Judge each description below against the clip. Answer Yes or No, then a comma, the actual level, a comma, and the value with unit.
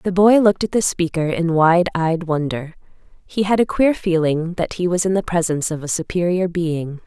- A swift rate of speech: Yes, fast, 210 wpm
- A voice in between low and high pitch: Yes, medium, 175 Hz